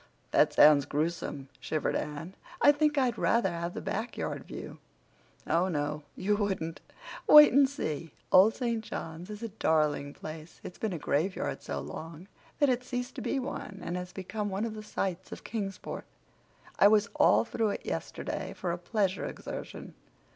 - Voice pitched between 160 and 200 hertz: Yes, high, 190 Hz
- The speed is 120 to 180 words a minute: Yes, average, 175 wpm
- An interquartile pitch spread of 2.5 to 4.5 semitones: No, wide, 5.6 semitones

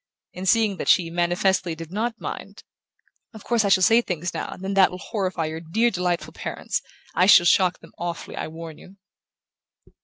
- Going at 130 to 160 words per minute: No, average, 190 wpm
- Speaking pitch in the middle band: Yes, medium, 180 Hz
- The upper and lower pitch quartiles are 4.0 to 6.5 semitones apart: No, average, 2.7 semitones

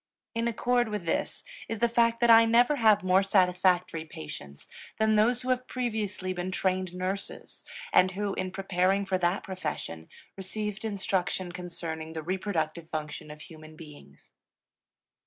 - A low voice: No, medium, 185 Hz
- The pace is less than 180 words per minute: Yes, average, 150 wpm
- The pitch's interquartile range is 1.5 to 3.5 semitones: No, average, 3.9 semitones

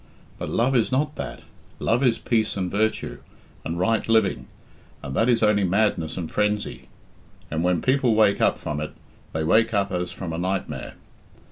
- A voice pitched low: Yes, low, 105 Hz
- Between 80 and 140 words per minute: No, average, 175 wpm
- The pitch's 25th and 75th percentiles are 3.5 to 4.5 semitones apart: Yes, average, 4.2 semitones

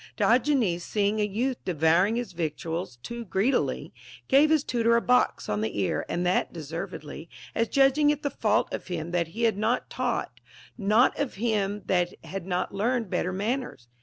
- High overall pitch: Yes, high, 205 Hz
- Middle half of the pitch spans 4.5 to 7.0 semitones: Yes, wide, 5.5 semitones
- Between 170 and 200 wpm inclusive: Yes, average, 175 wpm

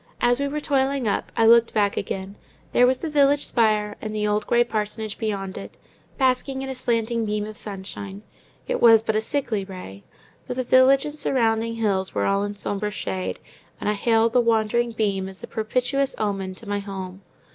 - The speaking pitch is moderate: No, high, 220 Hz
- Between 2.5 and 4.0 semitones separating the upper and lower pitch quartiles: Yes, average, 3.4 semitones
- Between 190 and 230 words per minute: Yes, average, 195 wpm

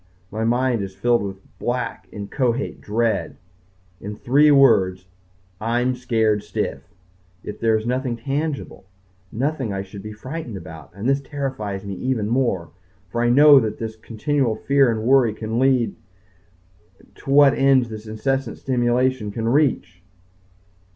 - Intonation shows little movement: No, average, 3.8 semitones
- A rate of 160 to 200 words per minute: No, average, 145 wpm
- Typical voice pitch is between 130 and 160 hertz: No, low, 120 Hz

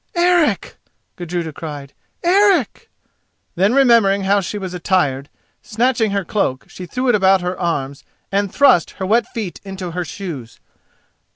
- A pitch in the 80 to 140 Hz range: No, high, 195 Hz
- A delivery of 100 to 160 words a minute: Yes, average, 145 wpm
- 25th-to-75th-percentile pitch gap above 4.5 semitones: Yes, average, 5.1 semitones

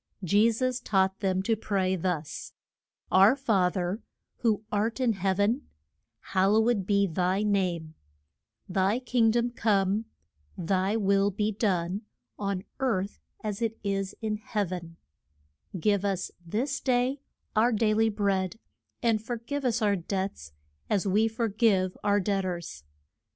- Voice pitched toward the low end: No, high, 205 Hz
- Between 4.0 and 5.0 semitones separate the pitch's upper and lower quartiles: No, average, 2.9 semitones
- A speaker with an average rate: Yes, average, 150 wpm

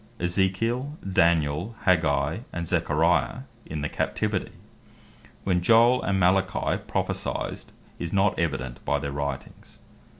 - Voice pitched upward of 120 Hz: No, very low, 85 Hz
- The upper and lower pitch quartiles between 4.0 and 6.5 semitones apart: Yes, average, 4.6 semitones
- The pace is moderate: No, slow, 110 wpm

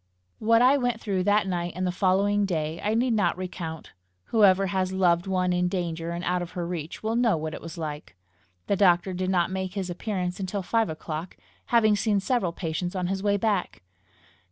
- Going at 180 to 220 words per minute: Yes, fast, 205 wpm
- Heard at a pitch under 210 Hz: Yes, medium, 185 Hz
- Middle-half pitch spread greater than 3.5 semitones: No, average, 2.8 semitones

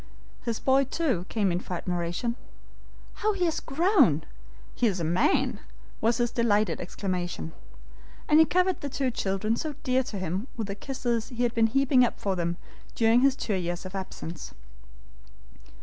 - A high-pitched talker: Yes, high, 225 Hz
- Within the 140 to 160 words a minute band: No, average, 170 wpm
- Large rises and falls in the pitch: Yes, wide, 6.2 semitones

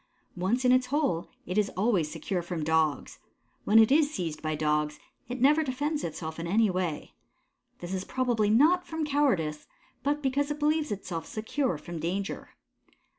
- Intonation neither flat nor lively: No, wide, 9.0 semitones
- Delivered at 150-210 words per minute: Yes, average, 170 wpm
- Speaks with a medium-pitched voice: No, high, 210 Hz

